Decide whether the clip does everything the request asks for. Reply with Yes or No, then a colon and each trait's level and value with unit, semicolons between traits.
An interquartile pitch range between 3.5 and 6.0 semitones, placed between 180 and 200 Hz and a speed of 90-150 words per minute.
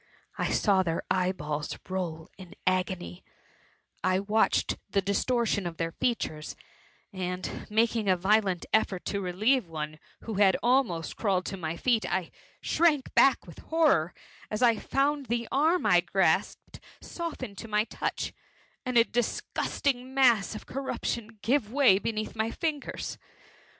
No: average, 5.2 semitones; high, 210 Hz; average, 145 wpm